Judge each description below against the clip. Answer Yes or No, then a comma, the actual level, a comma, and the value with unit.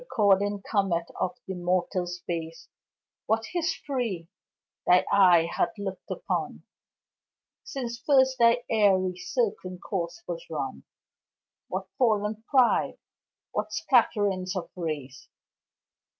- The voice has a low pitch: No, high, 200 Hz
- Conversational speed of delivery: No, slow, 105 wpm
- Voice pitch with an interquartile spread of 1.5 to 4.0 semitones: No, average, 4.9 semitones